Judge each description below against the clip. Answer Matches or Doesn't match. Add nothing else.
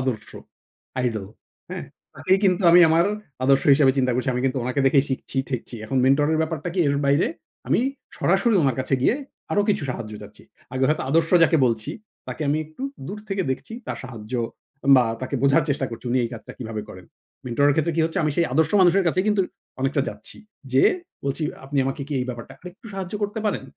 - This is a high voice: Doesn't match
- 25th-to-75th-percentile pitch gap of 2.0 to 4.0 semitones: Doesn't match